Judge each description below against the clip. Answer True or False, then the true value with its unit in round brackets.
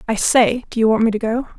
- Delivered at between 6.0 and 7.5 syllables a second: True (6.1 syllables/s)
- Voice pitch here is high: True (225 Hz)